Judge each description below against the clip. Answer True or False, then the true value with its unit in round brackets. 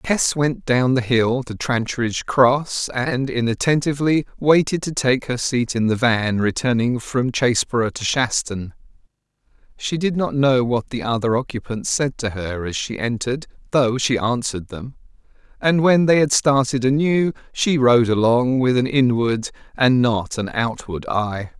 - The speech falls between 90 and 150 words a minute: False (160 wpm)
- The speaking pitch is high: False (125 Hz)